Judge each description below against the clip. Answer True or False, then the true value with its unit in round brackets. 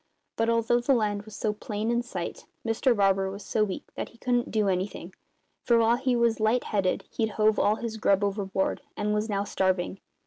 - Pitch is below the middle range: False (215 Hz)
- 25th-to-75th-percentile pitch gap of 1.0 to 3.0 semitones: True (2.7 semitones)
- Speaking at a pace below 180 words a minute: False (205 wpm)